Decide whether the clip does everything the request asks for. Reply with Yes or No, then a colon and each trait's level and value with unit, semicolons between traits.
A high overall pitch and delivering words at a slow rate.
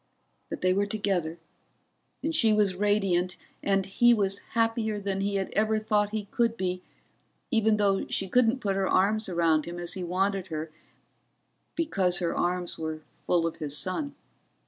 No: high, 195 Hz; average, 170 wpm